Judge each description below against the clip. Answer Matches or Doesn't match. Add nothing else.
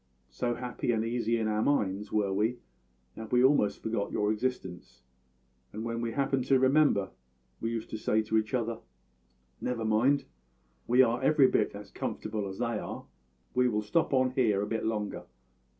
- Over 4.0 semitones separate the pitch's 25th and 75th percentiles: Doesn't match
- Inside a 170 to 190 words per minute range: Matches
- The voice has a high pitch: Doesn't match